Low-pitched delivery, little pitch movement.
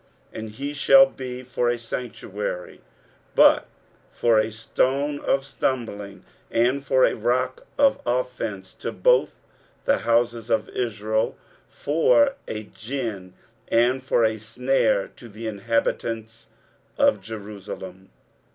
No: low, 115 Hz; average, 3.1 semitones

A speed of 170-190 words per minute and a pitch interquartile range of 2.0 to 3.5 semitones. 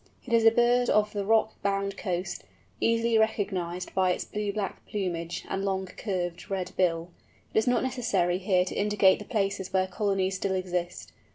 Yes: average, 180 wpm; narrow, 2.6 semitones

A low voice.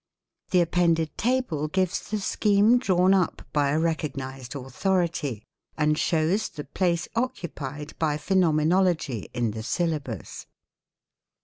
No: medium, 165 Hz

